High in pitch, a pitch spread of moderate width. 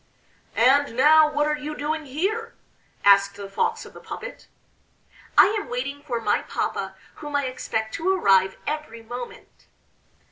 Yes: very high, 285 Hz; average, 4.9 semitones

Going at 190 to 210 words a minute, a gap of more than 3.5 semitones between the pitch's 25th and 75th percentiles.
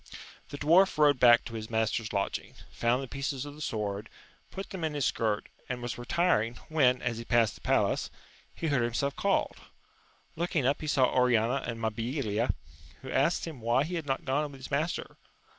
Yes: average, 195 wpm; average, 4.2 semitones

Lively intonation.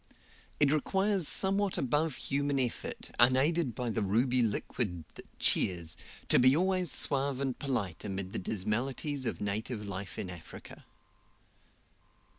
Yes: wide, 5.9 semitones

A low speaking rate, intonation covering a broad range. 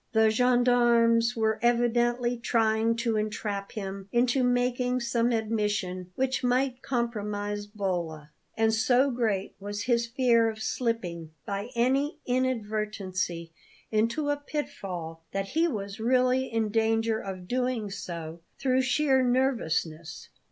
No: slow, 125 wpm; average, 3.3 semitones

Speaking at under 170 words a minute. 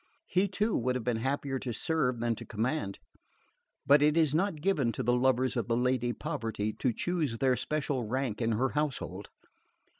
No: average, 185 wpm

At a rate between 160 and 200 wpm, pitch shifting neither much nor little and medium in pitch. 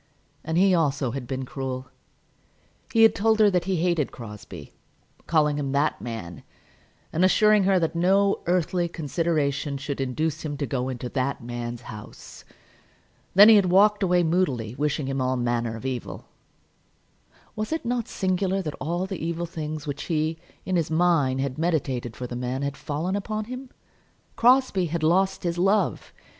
No: average, 170 wpm; wide, 5.8 semitones; medium, 160 Hz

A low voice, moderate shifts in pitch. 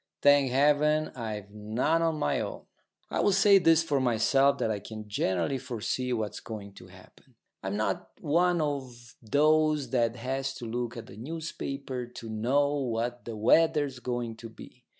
Yes: low, 125 Hz; average, 4.4 semitones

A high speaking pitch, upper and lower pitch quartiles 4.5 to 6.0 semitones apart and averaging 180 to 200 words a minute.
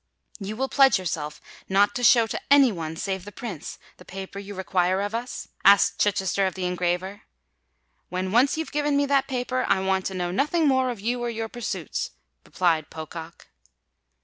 Yes: high, 200 Hz; average, 5.1 semitones; average, 185 wpm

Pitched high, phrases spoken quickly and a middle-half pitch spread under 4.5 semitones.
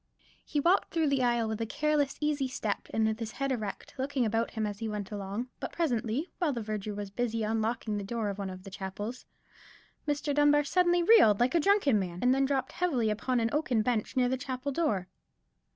No: high, 240 Hz; fast, 215 wpm; average, 5.0 semitones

